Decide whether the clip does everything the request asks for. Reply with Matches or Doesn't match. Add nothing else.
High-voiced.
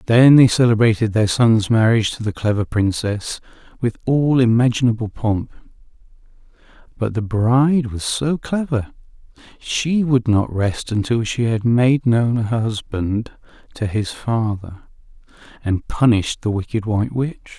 Doesn't match